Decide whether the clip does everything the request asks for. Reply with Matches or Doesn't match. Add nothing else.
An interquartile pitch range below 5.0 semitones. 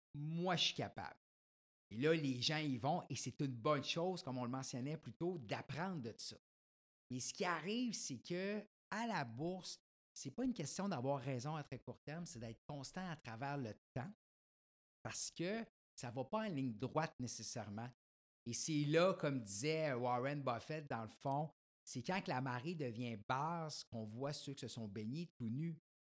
Doesn't match